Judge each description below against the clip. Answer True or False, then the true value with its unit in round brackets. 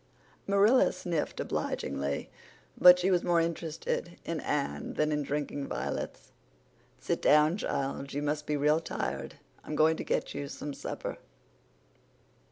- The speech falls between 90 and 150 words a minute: True (140 wpm)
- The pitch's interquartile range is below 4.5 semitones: True (2.8 semitones)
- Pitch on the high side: False (150 Hz)